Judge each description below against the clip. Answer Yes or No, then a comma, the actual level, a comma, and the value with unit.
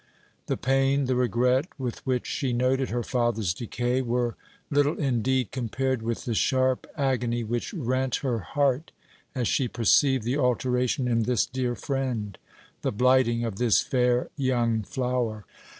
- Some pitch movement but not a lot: No, narrow, 1.9 semitones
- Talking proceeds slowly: No, average, 150 wpm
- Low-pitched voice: Yes, low, 125 Hz